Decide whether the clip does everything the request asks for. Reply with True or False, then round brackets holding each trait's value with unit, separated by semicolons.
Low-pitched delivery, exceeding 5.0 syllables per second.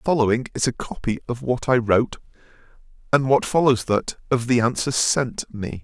True (125 Hz; 5.5 syllables/s)